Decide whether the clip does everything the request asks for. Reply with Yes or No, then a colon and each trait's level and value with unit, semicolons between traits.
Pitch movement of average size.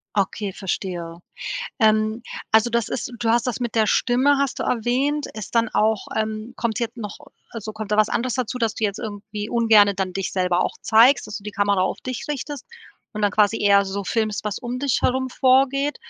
Yes: average, 3.0 semitones